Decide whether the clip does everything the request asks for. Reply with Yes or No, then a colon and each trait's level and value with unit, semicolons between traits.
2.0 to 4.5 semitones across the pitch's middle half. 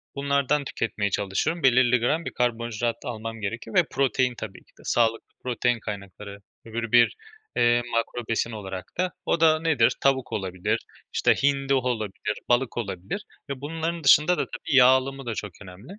Yes: average, 3.9 semitones